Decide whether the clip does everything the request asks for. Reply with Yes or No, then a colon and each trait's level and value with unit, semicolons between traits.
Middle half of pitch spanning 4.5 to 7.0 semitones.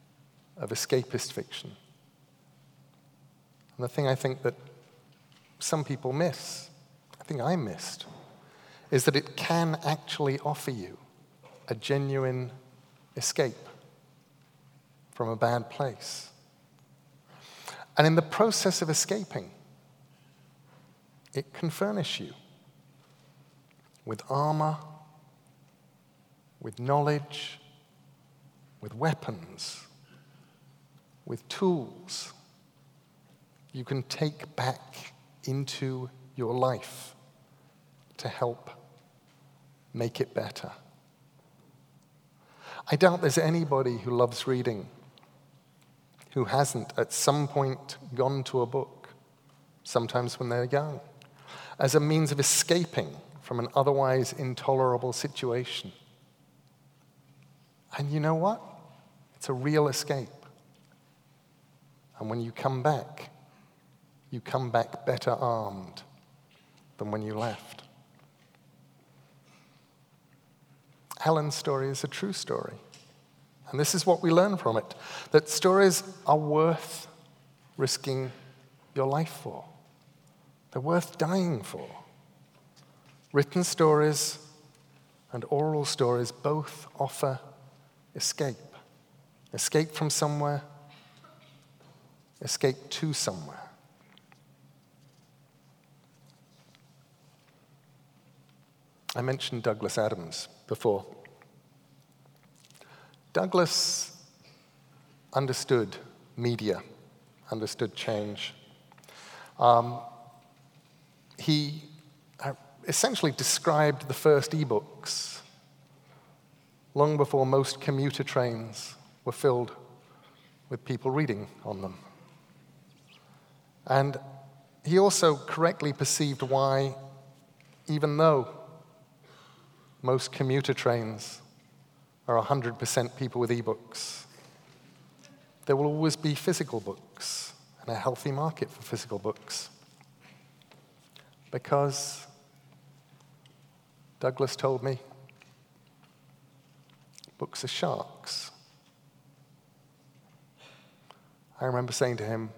No: average, 2.9 semitones